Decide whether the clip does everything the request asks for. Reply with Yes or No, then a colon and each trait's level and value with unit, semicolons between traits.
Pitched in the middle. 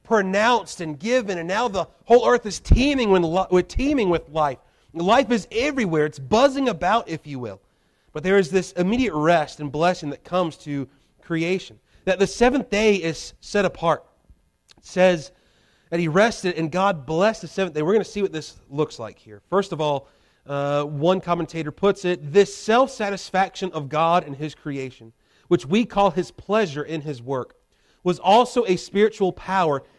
Yes: medium, 180 Hz